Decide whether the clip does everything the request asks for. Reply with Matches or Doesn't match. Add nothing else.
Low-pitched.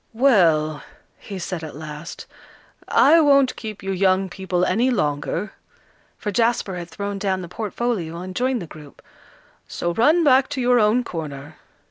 Doesn't match